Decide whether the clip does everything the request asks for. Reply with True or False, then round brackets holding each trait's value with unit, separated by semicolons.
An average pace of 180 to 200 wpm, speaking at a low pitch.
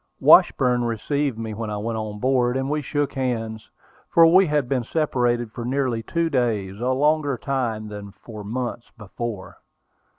False (165 wpm; 120 Hz)